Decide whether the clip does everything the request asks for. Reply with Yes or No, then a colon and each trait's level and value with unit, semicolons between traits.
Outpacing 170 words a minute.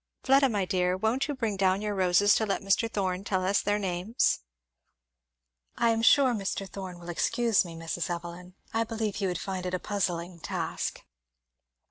Yes: average, 180 wpm